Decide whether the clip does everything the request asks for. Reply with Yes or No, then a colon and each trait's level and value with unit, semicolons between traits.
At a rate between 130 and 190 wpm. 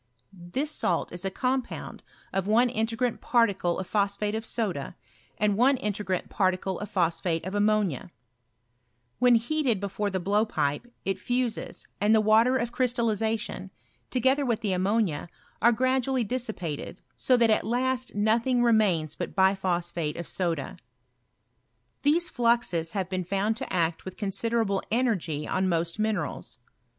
Yes: average, 140 wpm